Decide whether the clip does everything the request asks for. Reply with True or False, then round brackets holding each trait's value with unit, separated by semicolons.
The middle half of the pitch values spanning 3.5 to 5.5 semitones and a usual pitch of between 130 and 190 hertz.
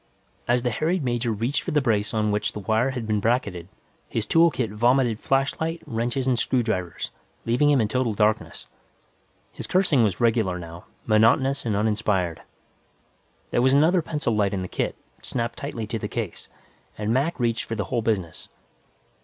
False (3.8 semitones; 115 Hz)